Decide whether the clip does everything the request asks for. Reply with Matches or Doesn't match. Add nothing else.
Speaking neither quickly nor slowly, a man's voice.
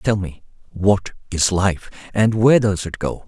Matches